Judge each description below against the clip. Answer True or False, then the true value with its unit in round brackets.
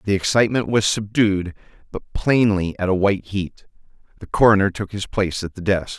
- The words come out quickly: False (180 wpm)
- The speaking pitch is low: True (100 Hz)